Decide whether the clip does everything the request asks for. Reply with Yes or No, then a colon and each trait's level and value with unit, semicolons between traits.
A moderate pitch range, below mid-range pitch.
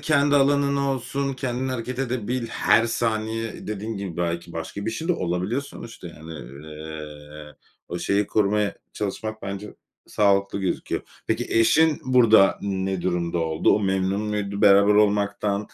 Yes: average, 3.9 semitones; low, 105 Hz